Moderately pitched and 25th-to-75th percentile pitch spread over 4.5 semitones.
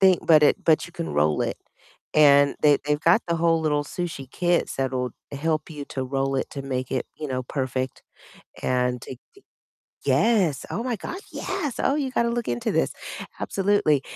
Yes: medium, 150 Hz; average, 5.1 semitones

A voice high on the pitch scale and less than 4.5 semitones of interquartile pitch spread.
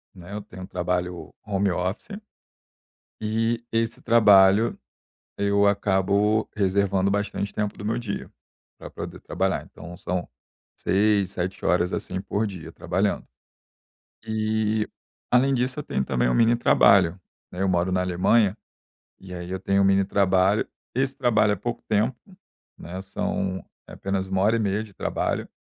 No: low, 100 Hz; average, 2.7 semitones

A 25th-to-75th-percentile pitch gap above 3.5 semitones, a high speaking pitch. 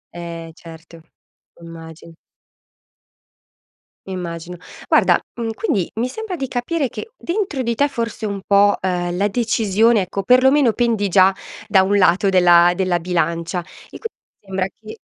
Yes: average, 5.1 semitones; high, 195 Hz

